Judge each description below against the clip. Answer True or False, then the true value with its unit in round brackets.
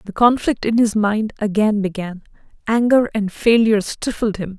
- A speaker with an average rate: True (155 wpm)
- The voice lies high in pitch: True (215 Hz)